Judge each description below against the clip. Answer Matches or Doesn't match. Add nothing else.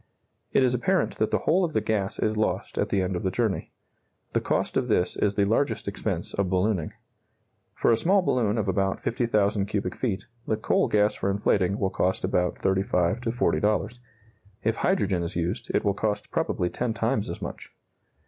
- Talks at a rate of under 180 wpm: Doesn't match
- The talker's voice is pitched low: Matches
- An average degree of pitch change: Matches